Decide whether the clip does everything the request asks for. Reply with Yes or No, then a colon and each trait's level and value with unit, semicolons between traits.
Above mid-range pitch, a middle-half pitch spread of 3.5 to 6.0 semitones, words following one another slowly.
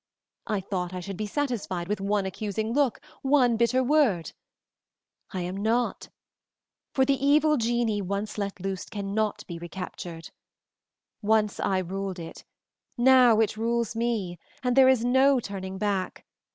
No: high, 215 Hz; average, 4.1 semitones; average, 145 wpm